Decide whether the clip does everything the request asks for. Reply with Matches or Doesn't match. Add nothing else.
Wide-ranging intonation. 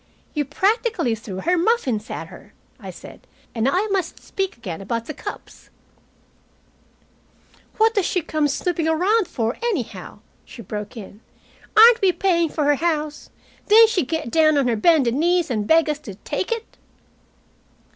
Matches